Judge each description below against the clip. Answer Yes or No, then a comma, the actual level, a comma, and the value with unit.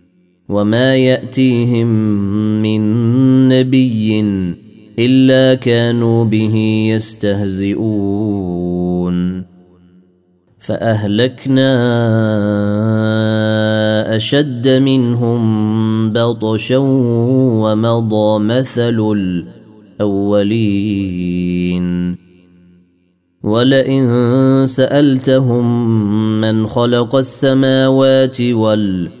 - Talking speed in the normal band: No, slow, 45 wpm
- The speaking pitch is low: Yes, low, 110 Hz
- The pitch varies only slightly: No, average, 3.1 semitones